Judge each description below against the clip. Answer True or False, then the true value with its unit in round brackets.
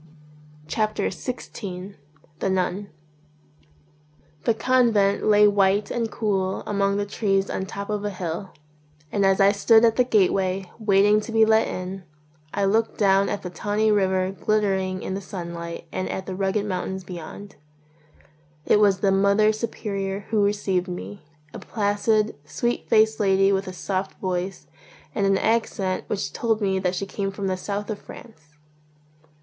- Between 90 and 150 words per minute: False (165 wpm)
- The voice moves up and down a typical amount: False (1.9 semitones)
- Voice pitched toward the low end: False (200 Hz)